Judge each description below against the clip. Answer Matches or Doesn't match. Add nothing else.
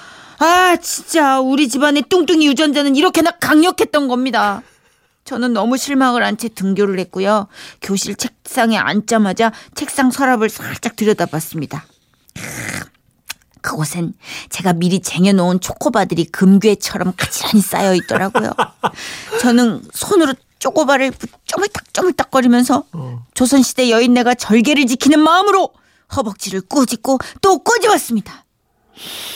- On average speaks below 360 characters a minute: Matches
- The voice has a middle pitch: Doesn't match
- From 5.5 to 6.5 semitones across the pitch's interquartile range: Doesn't match